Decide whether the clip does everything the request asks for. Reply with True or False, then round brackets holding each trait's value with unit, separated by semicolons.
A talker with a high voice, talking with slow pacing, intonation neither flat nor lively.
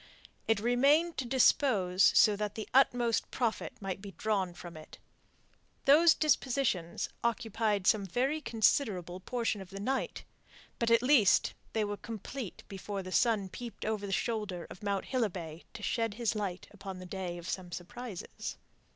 False (210 Hz; 160 wpm; 4.2 semitones)